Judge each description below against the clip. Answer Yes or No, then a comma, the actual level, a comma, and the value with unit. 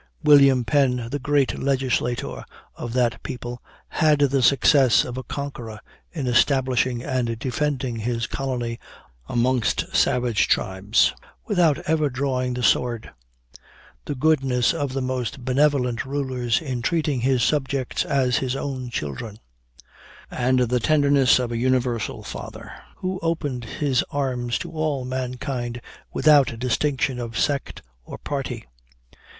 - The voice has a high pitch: No, low, 130 Hz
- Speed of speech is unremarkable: No, slow, 130 wpm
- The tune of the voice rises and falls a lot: No, narrow, 2.5 semitones